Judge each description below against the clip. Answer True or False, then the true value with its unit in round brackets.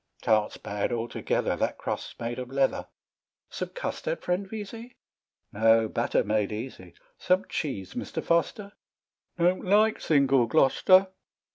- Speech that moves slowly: True (130 wpm)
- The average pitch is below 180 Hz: True (135 Hz)